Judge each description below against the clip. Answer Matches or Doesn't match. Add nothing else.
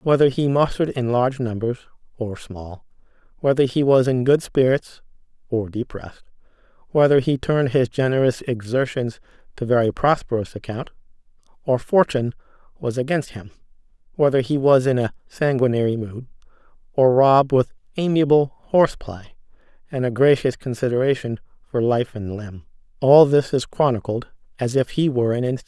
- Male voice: Matches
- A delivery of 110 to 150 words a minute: Matches